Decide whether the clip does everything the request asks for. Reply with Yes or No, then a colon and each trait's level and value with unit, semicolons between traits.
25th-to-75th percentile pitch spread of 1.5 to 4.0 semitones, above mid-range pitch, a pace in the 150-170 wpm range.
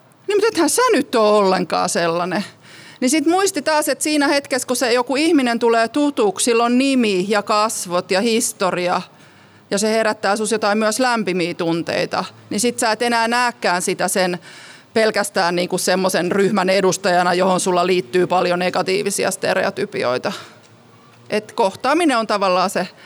No: average, 5.3 semitones; high, 205 Hz; fast, 155 wpm